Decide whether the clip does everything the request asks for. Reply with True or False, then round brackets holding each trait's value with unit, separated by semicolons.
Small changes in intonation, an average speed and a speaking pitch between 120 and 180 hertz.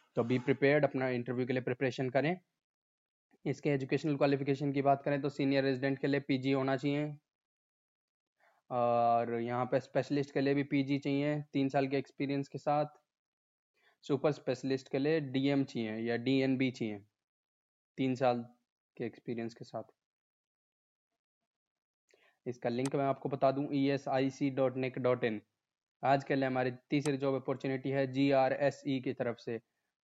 True (1.7 semitones; 130 wpm; 135 Hz)